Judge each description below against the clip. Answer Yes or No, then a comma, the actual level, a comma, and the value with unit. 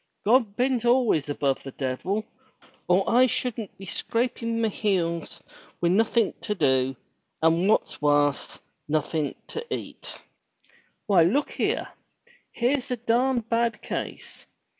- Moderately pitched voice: No, high, 210 Hz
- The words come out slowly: Yes, slow, 125 wpm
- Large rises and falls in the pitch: Yes, wide, 6.6 semitones